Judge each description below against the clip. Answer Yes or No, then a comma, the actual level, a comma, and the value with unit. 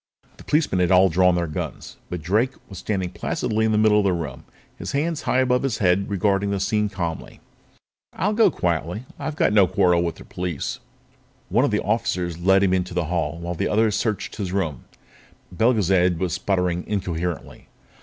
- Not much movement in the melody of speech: No, average, 3.4 semitones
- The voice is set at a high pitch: No, very low, 95 Hz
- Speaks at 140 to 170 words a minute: No, average, 200 wpm